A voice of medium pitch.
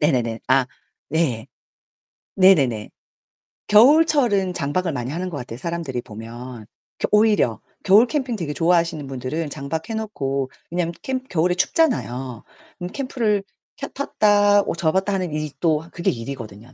Yes: medium, 165 Hz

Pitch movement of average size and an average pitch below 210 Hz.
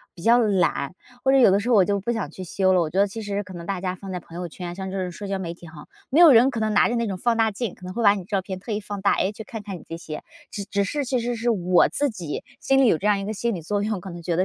Yes: average, 3.6 semitones; high, 200 Hz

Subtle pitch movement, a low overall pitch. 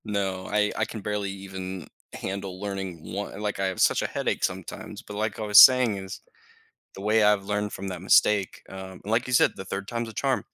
Yes: narrow, 1.7 semitones; low, 100 Hz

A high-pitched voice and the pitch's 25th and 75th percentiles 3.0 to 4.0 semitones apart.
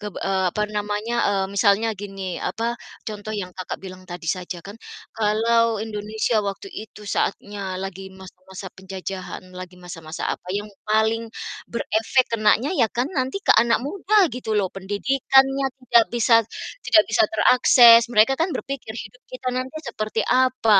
Yes: high, 215 Hz; average, 3.5 semitones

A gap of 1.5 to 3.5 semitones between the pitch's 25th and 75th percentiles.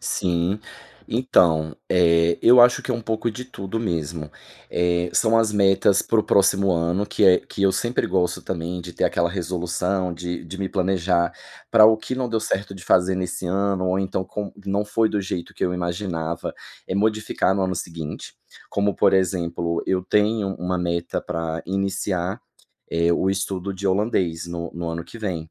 Yes: average, 2.8 semitones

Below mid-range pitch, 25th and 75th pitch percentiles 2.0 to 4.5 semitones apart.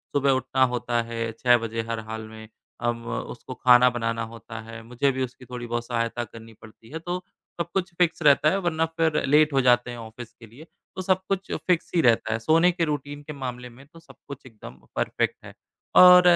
No: low, 125 Hz; average, 5.1 semitones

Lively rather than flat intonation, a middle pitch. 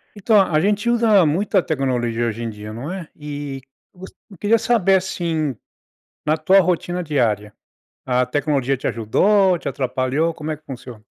Yes: wide, 6.7 semitones; medium, 155 Hz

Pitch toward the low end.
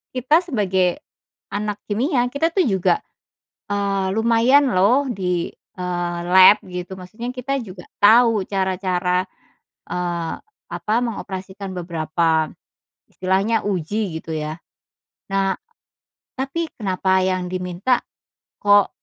No: high, 195 Hz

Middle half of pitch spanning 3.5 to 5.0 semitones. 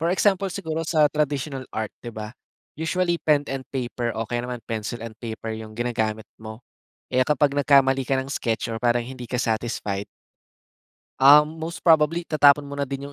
Yes: average, 4.4 semitones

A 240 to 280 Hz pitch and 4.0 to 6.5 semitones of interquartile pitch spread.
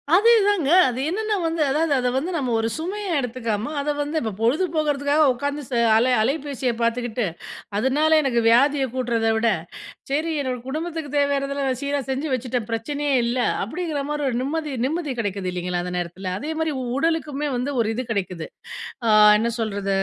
Yes: very high, 275 Hz; average, 4.6 semitones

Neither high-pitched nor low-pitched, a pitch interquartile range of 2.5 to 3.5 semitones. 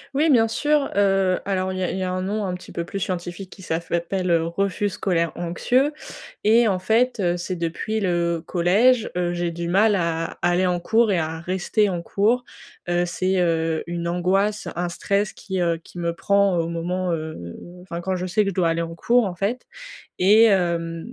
Yes: medium, 180 Hz; average, 2.8 semitones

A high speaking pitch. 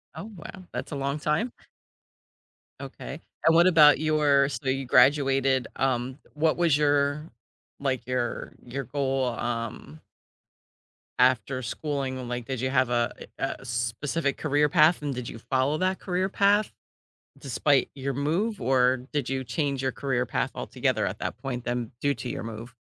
No: low, 135 Hz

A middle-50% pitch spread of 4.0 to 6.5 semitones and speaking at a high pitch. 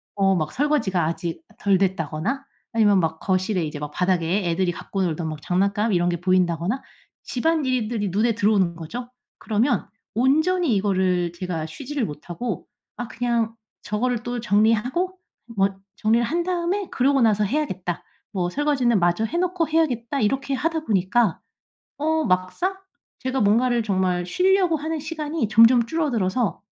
No: wide, 7.0 semitones; high, 220 Hz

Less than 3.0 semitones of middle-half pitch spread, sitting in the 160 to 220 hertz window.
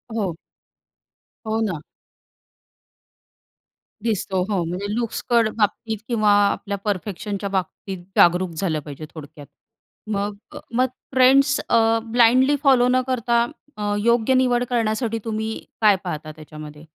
No: average, 4.5 semitones; high, 215 Hz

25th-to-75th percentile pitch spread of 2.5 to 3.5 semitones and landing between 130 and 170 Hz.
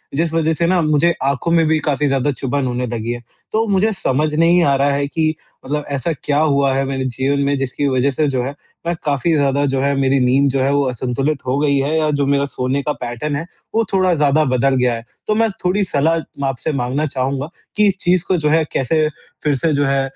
Yes: average, 2.9 semitones; medium, 140 Hz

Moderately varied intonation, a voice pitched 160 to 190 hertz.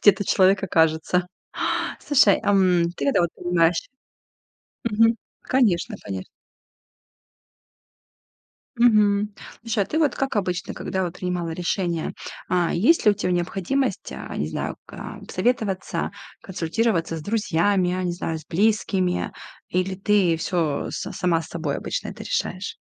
Yes: average, 3.5 semitones; medium, 185 Hz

